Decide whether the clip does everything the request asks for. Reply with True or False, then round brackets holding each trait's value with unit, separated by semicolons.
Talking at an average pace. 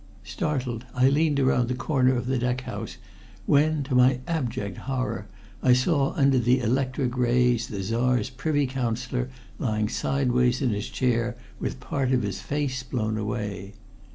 True (155 wpm)